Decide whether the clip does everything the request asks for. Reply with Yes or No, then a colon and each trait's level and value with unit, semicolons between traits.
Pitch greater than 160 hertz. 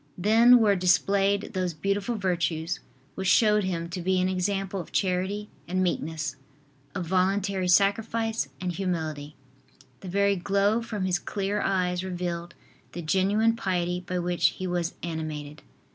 Yes: medium, 185 Hz